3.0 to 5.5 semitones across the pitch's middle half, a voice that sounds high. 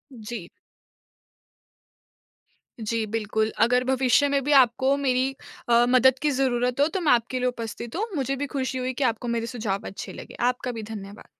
No: narrow, 2.6 semitones; very high, 250 Hz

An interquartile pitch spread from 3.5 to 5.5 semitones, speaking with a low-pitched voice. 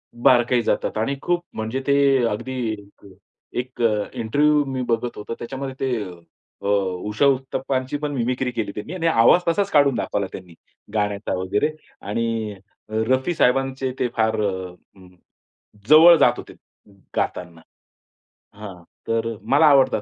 Yes: average, 4.1 semitones; low, 125 Hz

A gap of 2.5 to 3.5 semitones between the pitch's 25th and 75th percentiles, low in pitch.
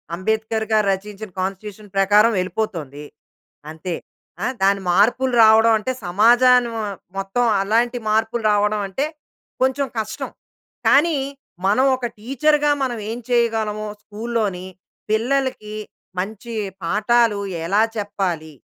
No: average, 3.2 semitones; high, 215 Hz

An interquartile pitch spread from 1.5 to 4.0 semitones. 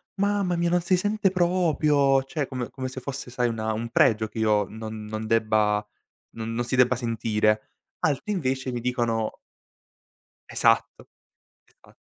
No: wide, 5.5 semitones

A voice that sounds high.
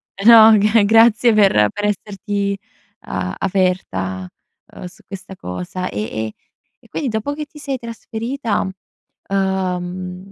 Yes: high, 195 Hz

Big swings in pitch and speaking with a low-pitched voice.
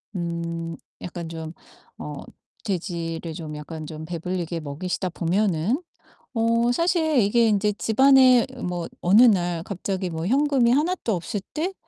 No: wide, 5.9 semitones; medium, 185 Hz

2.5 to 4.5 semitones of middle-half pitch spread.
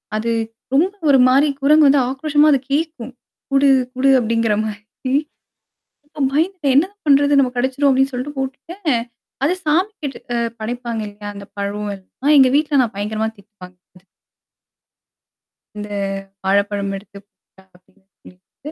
No: wide, 5.5 semitones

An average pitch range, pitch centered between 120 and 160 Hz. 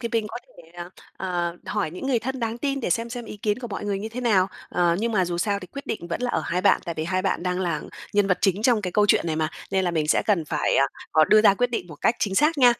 No: average, 4.8 semitones; high, 200 Hz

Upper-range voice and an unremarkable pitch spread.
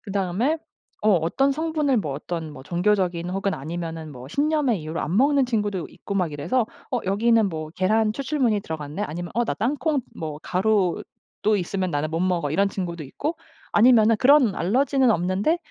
No: high, 195 Hz; wide, 6.4 semitones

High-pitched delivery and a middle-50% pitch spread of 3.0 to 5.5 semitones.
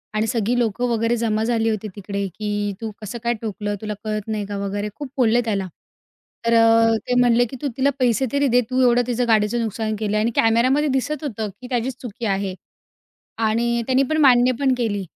No: high, 230 Hz; narrow, 2.6 semitones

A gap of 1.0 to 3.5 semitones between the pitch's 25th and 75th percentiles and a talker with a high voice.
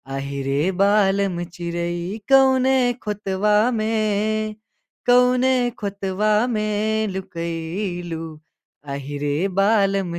No: average, 3.9 semitones; high, 200 Hz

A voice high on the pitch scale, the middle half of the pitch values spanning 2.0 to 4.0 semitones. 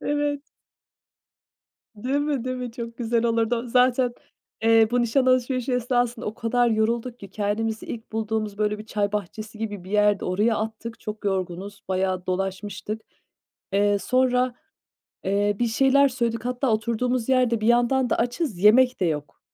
Yes: high, 230 Hz; average, 3.1 semitones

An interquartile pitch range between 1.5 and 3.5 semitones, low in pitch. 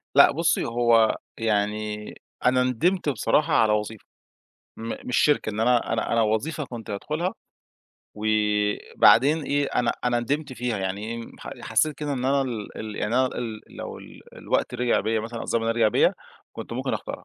Yes: average, 3.1 semitones; low, 115 Hz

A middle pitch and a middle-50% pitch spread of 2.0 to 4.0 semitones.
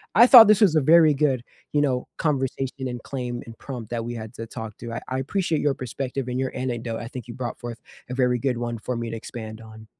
No: low, 125 Hz; average, 2.8 semitones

